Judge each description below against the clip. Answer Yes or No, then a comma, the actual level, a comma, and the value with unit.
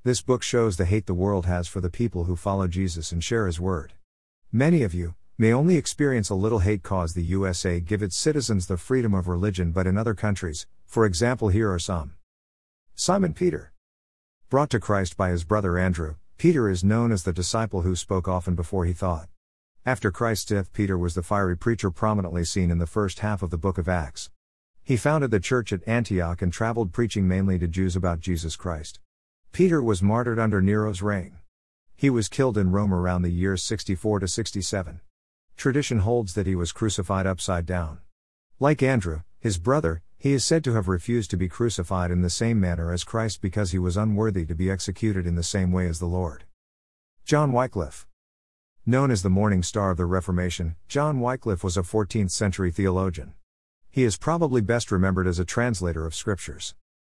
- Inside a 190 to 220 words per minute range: Yes, average, 195 wpm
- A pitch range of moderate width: Yes, average, 4.0 semitones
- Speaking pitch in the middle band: No, very low, 95 Hz